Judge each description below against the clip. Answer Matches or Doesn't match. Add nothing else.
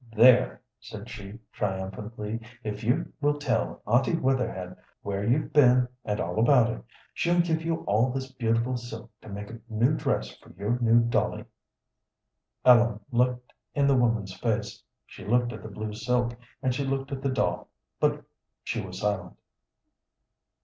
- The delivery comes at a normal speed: Matches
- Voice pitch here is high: Doesn't match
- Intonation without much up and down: Doesn't match